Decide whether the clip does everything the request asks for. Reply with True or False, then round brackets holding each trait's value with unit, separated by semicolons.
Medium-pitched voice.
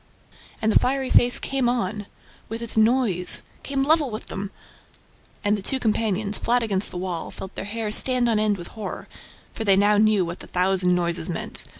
False (215 Hz)